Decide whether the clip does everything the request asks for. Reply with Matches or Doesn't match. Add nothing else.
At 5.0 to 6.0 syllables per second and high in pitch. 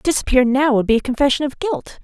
Doesn't match